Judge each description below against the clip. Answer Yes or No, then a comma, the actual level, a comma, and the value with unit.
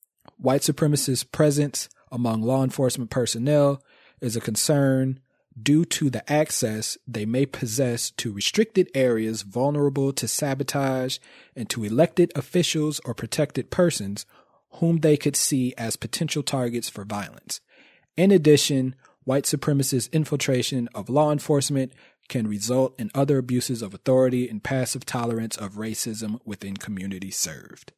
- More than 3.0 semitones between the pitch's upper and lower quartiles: Yes, average, 4.0 semitones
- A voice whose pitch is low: Yes, low, 130 Hz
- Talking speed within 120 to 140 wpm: Yes, slow, 135 wpm